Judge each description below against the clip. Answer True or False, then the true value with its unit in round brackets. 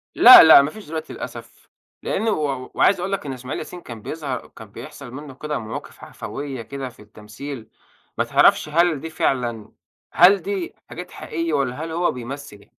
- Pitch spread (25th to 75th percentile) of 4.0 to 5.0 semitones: True (4.6 semitones)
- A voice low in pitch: False (145 Hz)